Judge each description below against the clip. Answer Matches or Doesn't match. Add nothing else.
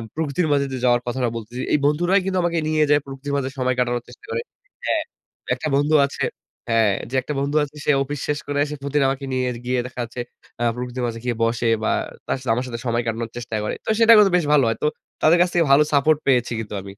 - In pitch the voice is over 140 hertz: Doesn't match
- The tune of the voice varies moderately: Matches